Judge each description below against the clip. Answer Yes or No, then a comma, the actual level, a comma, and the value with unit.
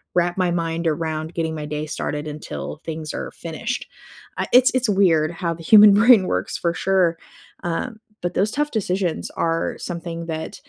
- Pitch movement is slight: No, average, 3.2 semitones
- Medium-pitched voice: Yes, medium, 170 Hz